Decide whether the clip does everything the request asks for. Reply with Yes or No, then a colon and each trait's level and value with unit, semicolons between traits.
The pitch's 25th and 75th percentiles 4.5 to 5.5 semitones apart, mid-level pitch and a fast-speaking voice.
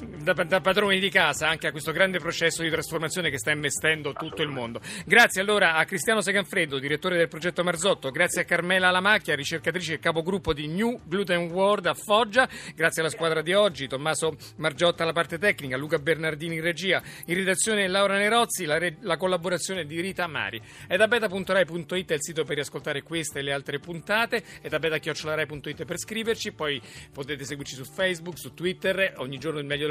No: average, 3.6 semitones; medium, 170 Hz; fast, 185 wpm